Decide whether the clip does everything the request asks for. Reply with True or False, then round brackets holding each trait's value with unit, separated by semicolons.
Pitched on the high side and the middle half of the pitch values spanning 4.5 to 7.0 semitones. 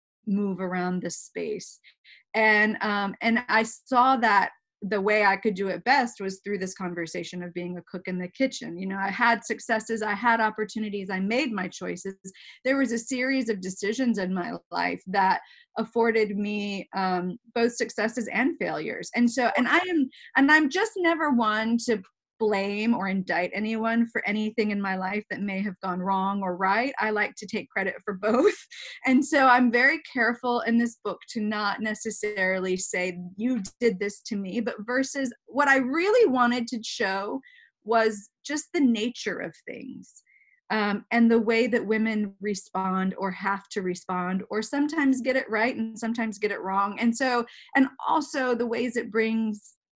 False (220 Hz; 3.7 semitones)